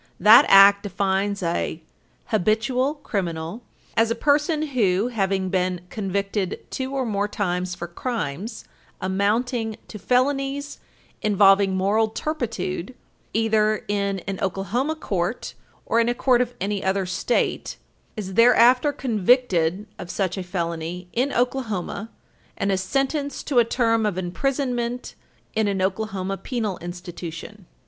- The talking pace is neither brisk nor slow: No, slow, 130 wpm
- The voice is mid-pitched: No, high, 205 Hz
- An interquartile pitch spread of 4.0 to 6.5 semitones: Yes, average, 4.4 semitones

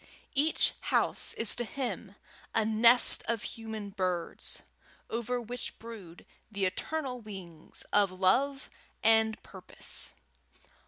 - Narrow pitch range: No, average, 3.7 semitones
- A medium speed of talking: No, slow, 110 wpm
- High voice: Yes, high, 220 Hz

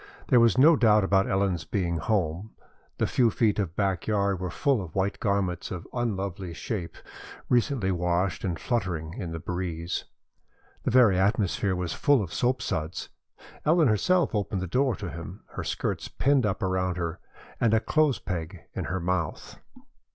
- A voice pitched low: Yes, very low, 95 Hz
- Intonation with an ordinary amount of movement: Yes, average, 4.2 semitones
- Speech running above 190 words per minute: No, average, 170 wpm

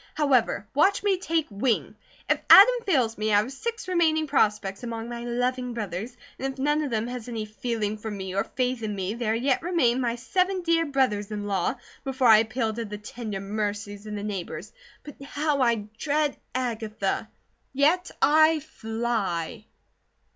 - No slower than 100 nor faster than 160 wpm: No, average, 175 wpm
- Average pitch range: Yes, average, 4.9 semitones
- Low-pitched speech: No, high, 235 Hz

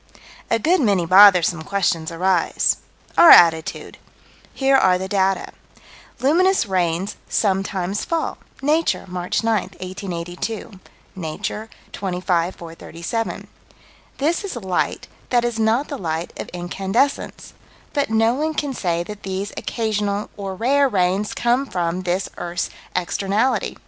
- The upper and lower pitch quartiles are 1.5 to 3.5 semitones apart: No, average, 4.5 semitones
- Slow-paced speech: Yes, slow, 125 wpm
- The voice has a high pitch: Yes, high, 195 Hz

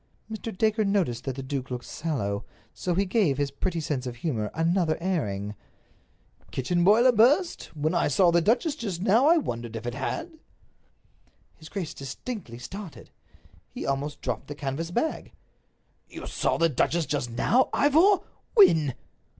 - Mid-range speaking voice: Yes, medium, 165 Hz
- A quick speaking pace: No, average, 160 wpm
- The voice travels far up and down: Yes, wide, 8.2 semitones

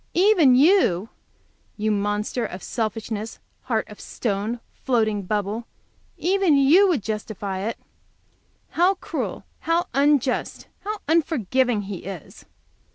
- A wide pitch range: Yes, wide, 6.9 semitones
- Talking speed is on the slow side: Yes, slow, 110 wpm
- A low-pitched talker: No, high, 230 Hz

